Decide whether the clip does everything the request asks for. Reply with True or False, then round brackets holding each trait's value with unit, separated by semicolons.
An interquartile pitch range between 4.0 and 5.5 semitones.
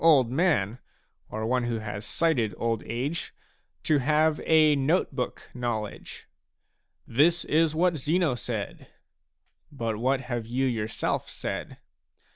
True (5.2 semitones)